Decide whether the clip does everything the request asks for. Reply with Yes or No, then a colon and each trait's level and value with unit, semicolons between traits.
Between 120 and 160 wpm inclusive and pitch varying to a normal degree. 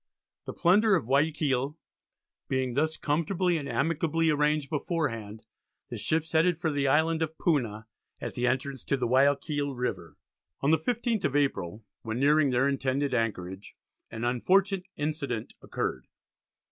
Yes: average, 140 wpm; average, 4.4 semitones